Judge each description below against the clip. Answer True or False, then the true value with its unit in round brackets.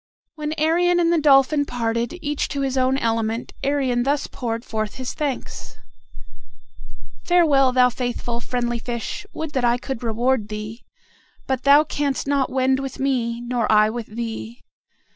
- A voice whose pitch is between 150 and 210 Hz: False (255 Hz)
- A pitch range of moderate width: True (3.2 semitones)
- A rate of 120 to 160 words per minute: True (155 wpm)